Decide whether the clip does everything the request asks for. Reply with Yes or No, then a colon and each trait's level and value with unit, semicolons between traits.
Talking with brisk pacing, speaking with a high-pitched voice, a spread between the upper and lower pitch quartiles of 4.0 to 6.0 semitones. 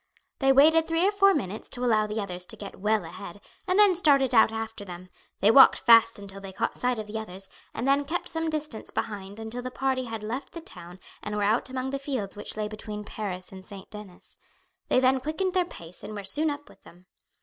Yes: fast, 230 wpm; high, 225 Hz; average, 5.3 semitones